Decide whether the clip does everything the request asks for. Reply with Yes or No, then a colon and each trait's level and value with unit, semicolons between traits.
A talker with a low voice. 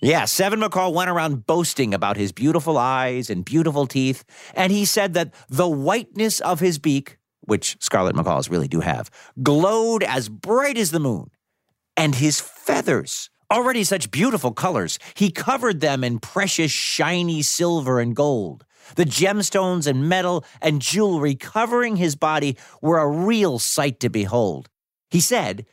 No: medium, 160 Hz